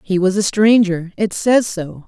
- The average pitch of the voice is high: Yes, high, 195 Hz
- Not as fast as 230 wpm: Yes, average, 200 wpm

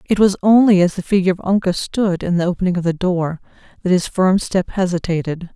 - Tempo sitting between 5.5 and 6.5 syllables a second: Yes, 5.9 syllables/s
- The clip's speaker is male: No, female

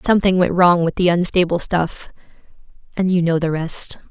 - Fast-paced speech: No, average, 160 wpm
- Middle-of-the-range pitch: Yes, medium, 175 Hz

